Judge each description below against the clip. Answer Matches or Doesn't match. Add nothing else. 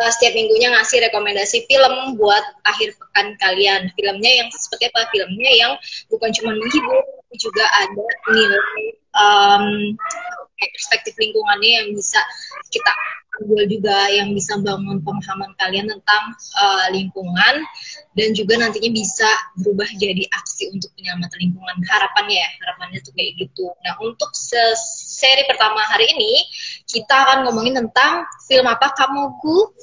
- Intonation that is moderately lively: Matches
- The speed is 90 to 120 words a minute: Doesn't match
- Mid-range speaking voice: Doesn't match